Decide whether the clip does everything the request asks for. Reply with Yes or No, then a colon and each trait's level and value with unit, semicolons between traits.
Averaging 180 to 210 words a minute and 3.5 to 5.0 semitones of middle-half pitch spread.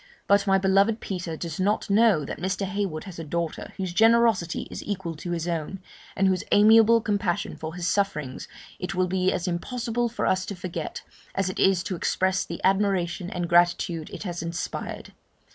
No: average, 185 wpm; average, 2.7 semitones